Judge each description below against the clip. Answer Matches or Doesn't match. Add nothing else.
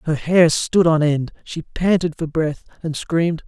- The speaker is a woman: Doesn't match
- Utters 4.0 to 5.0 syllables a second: Matches